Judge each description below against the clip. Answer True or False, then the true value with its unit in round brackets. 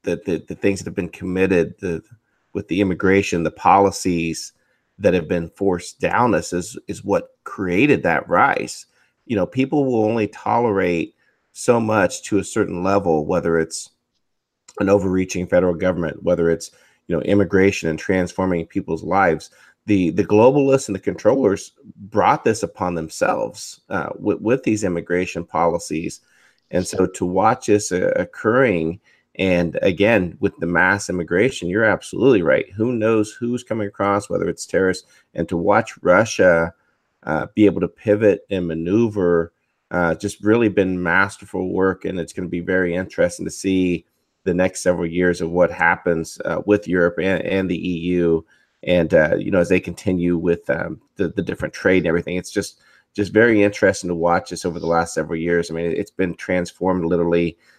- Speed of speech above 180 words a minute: False (175 wpm)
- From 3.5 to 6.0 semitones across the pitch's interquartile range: False (2.8 semitones)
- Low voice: True (90 Hz)